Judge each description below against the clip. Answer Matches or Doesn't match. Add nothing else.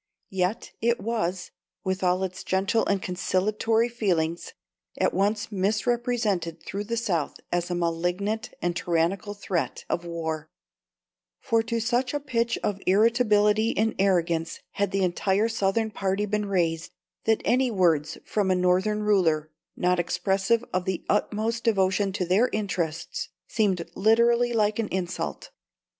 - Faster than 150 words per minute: Doesn't match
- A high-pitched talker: Matches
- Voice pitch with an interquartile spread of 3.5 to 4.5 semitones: Matches